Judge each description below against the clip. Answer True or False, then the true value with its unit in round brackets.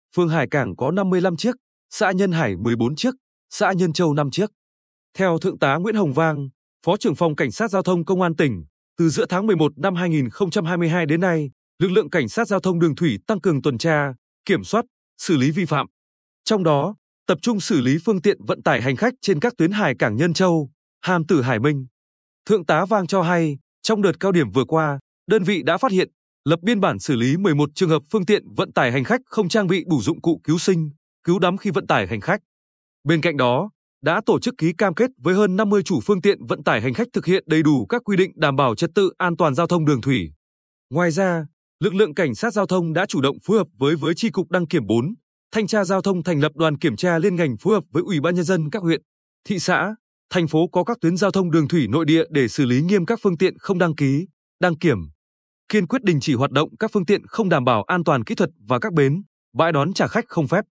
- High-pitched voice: False (175 Hz)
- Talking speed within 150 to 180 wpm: False (250 wpm)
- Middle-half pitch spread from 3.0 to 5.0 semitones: True (4.6 semitones)